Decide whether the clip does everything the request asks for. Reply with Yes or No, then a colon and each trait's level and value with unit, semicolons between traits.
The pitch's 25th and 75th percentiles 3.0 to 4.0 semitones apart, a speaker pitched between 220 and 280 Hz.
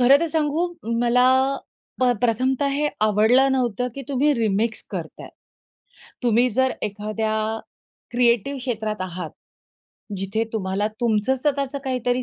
Yes: average, 3.6 semitones; high, 245 Hz